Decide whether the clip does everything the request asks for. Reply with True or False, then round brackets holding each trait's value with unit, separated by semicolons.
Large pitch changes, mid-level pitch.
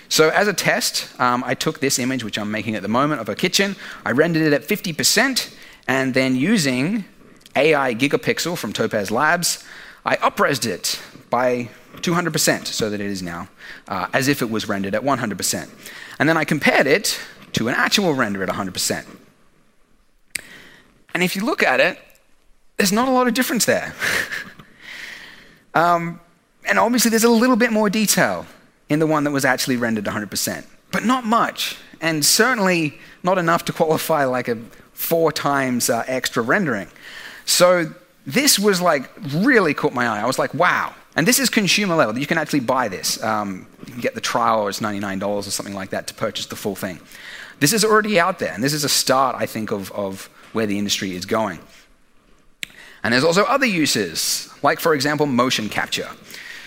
True (8.2 semitones; 155 Hz)